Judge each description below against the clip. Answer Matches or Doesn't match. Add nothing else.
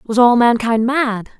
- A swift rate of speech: Doesn't match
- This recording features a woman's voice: Matches